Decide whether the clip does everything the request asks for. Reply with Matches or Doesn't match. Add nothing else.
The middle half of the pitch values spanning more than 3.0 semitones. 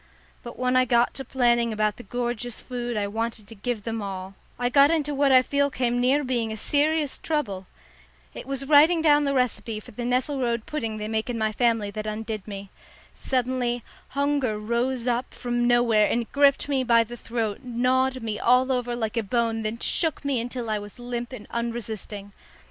Doesn't match